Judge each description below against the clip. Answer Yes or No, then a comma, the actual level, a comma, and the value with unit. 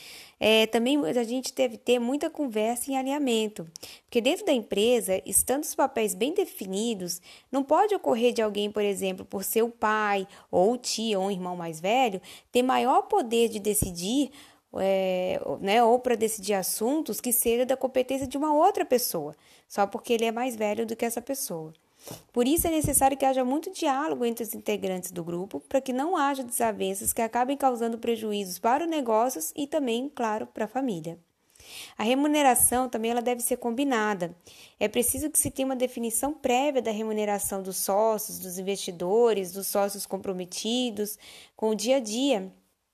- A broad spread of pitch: No, average, 4.4 semitones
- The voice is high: Yes, high, 235 Hz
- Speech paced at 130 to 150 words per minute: No, average, 175 wpm